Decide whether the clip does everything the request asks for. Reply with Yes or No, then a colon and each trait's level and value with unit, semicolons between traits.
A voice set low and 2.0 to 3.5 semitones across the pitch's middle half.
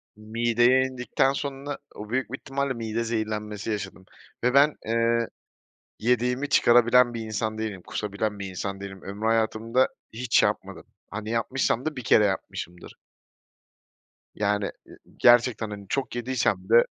Yes: low, 115 Hz; average, 2.9 semitones